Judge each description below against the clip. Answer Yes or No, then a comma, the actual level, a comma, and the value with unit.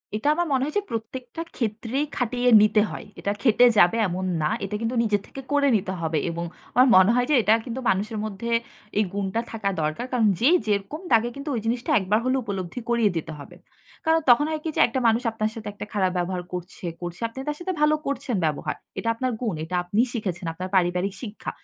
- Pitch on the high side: Yes, high, 220 Hz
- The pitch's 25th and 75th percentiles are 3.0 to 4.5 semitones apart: No, average, 4.9 semitones